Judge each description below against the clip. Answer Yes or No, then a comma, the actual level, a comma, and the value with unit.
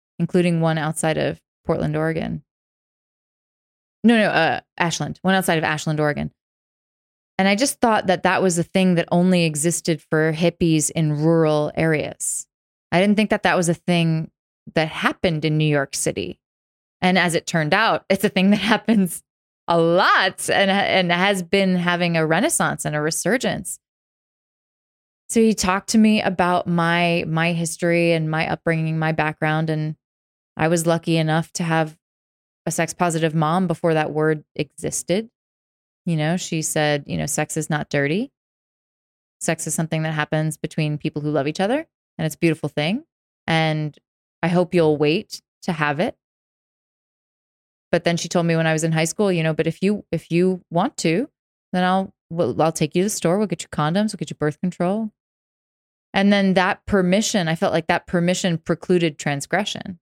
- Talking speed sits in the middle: Yes, average, 180 wpm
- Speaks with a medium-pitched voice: Yes, medium, 170 Hz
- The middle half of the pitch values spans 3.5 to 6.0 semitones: No, average, 3.0 semitones